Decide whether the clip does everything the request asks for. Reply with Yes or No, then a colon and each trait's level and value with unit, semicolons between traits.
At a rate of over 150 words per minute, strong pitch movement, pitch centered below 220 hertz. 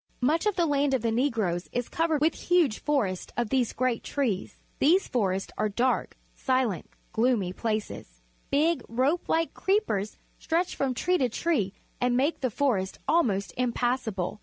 No: average, 160 wpm; wide, 5.7 semitones; very high, 250 Hz